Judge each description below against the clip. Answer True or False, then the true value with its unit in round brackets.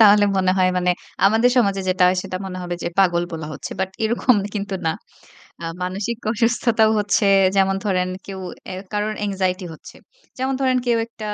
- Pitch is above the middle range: True (195 Hz)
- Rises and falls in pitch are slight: False (3.2 semitones)